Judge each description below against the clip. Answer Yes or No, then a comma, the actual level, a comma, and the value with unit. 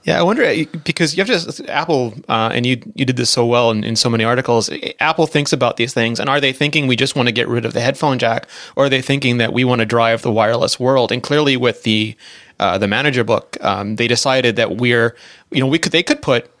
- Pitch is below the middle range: Yes, low, 125 Hz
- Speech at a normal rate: No, fast, 260 wpm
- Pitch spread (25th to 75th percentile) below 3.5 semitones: Yes, average, 2.9 semitones